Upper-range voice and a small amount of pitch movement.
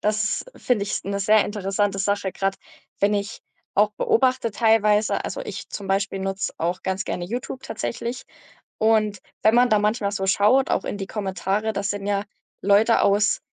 Yes: high, 205 Hz; narrow, 1.9 semitones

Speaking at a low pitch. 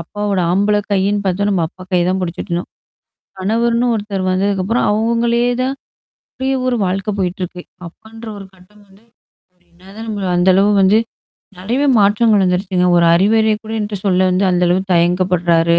No: high, 195 Hz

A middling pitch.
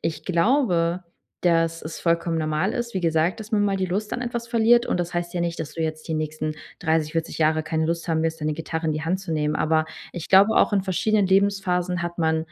Yes: medium, 170 Hz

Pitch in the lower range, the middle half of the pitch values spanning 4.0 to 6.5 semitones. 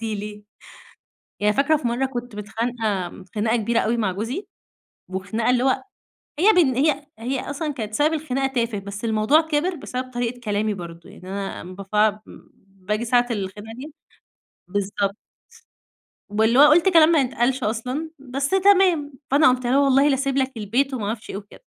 No: high, 240 Hz; average, 4.8 semitones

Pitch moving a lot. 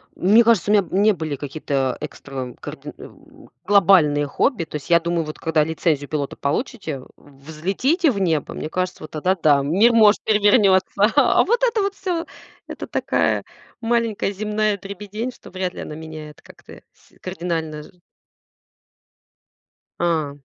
Yes: wide, 5.7 semitones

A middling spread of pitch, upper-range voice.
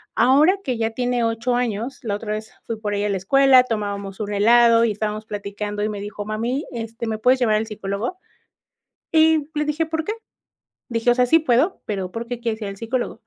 Yes: average, 3.2 semitones; high, 230 Hz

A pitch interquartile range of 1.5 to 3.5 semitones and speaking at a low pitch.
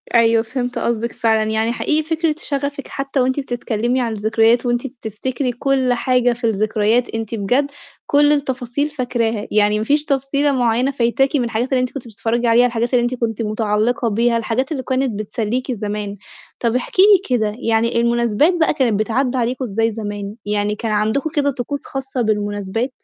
No: average, 3.1 semitones; high, 240 Hz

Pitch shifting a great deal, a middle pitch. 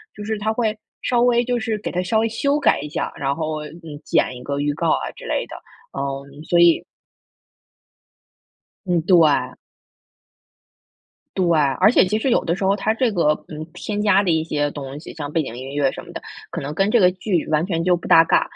Yes: wide, 6.1 semitones; medium, 175 Hz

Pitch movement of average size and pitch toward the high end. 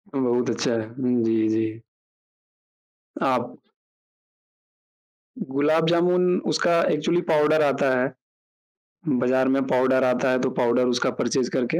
No: average, 3.4 semitones; low, 130 Hz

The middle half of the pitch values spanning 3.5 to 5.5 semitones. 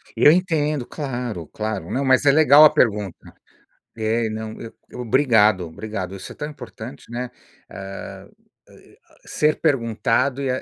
Yes: average, 4.5 semitones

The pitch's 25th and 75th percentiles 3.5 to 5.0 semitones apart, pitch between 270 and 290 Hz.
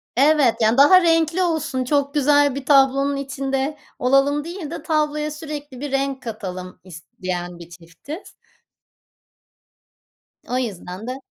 Yes: average, 4.0 semitones; very high, 275 Hz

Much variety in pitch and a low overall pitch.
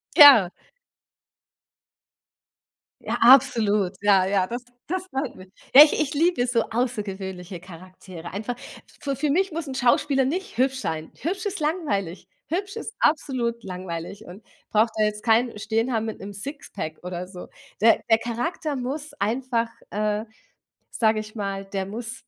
No: wide, 5.8 semitones; high, 230 Hz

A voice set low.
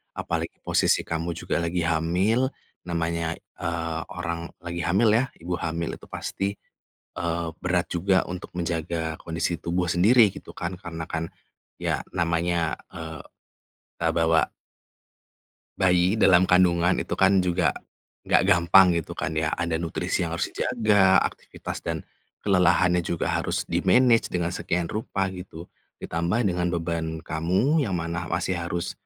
Yes: very low, 85 Hz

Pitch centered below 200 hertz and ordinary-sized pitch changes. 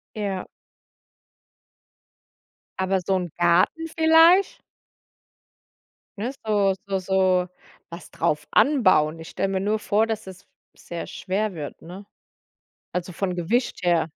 Yes: high, 190 Hz; average, 3.5 semitones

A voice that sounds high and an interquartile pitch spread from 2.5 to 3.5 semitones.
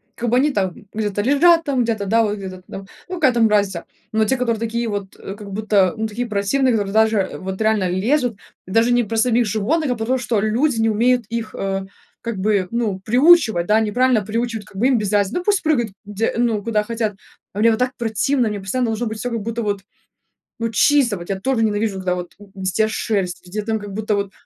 Yes: high, 220 Hz; average, 2.9 semitones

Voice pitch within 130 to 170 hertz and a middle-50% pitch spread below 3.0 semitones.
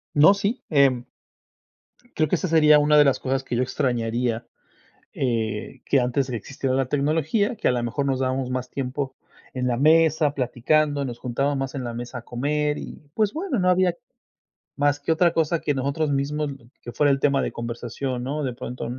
No: medium, 140 Hz; average, 3.3 semitones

